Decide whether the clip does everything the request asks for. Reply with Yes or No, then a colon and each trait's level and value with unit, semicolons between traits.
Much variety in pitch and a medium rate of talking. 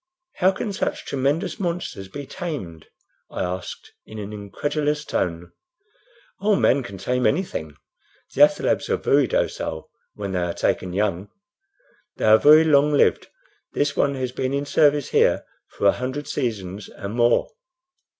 Yes: wide, 6.8 semitones; average, 150 wpm